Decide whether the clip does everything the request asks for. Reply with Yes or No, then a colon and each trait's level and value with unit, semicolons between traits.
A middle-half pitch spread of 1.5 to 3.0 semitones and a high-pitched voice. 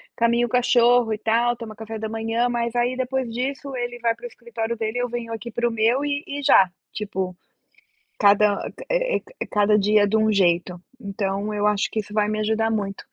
Yes: narrow, 2.6 semitones; high, 225 Hz